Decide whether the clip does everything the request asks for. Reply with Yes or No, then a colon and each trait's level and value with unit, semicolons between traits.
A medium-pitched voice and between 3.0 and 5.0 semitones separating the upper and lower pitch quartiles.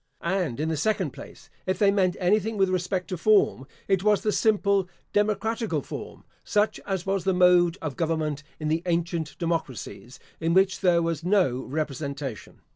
Yes: medium, 180 Hz; average, 3.7 semitones